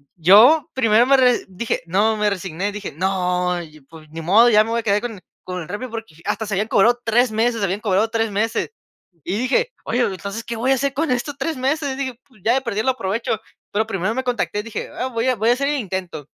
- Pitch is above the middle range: Yes, high, 220 Hz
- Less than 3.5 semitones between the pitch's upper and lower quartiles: No, average, 4.3 semitones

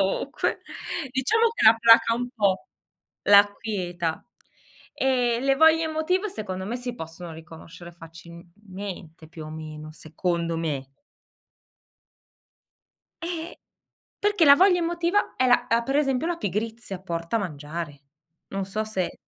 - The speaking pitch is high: Yes, high, 205 Hz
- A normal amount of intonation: No, wide, 7.9 semitones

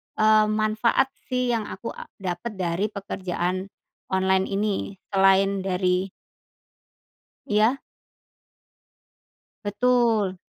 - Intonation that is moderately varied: No, narrow, 2.3 semitones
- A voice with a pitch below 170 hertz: No, high, 200 Hz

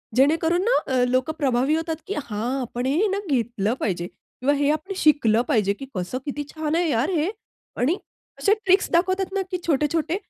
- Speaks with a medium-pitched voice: No, very high, 295 Hz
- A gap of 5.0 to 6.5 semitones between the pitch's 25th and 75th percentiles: Yes, wide, 5.5 semitones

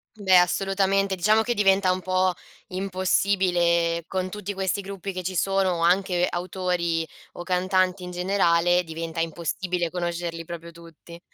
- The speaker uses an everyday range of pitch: No, narrow, 2.0 semitones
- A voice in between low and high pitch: Yes, medium, 180 Hz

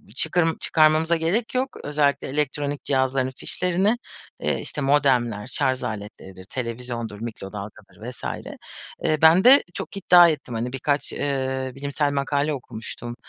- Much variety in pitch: No, average, 4.4 semitones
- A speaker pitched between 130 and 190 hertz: Yes, medium, 140 Hz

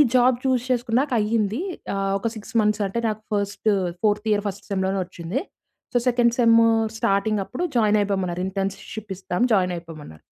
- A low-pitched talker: No, high, 210 Hz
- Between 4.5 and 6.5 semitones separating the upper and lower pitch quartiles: No, average, 2.9 semitones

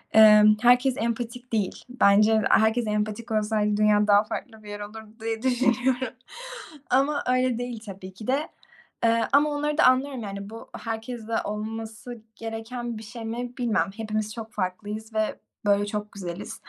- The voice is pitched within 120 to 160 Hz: No, high, 225 Hz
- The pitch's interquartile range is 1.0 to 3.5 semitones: Yes, narrow, 2.6 semitones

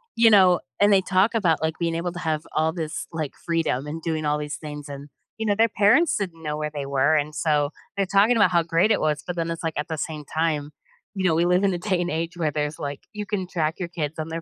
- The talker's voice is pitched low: No, medium, 165 Hz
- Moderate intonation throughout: Yes, average, 3.4 semitones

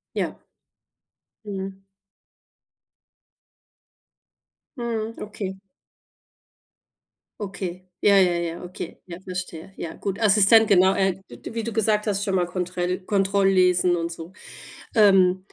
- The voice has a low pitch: No, high, 190 Hz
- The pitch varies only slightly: Yes, narrow, 2.1 semitones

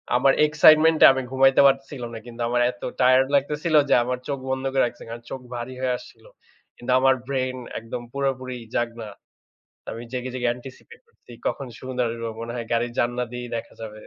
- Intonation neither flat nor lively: No, narrow, 2.0 semitones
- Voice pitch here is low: Yes, low, 130 Hz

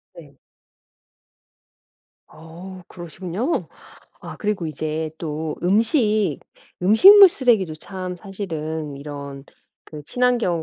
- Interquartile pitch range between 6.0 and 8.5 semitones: No, average, 5.2 semitones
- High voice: No, medium, 175 Hz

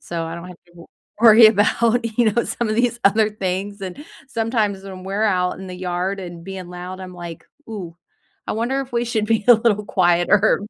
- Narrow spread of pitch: No, average, 3.7 semitones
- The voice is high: Yes, high, 200 Hz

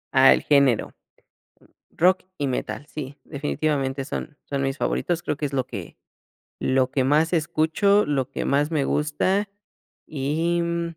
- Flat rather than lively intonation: No, average, 3.3 semitones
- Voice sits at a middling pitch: Yes, medium, 150 Hz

